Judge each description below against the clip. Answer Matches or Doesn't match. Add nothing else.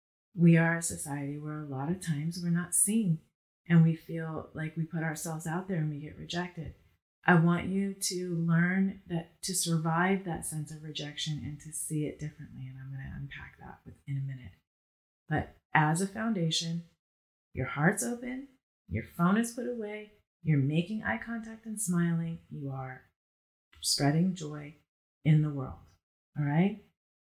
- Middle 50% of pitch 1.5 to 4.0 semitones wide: Matches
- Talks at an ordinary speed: Matches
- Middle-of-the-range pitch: Matches